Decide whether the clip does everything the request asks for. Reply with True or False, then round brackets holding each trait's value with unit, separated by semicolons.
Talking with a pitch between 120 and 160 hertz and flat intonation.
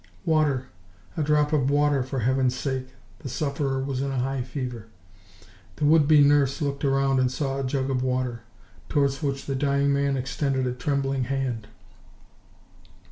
True (135 Hz; 1.6 semitones)